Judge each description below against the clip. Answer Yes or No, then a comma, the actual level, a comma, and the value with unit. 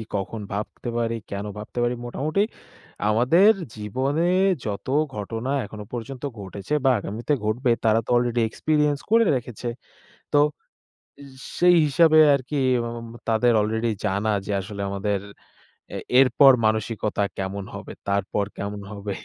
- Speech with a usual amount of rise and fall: Yes, average, 4.4 semitones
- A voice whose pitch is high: No, low, 115 Hz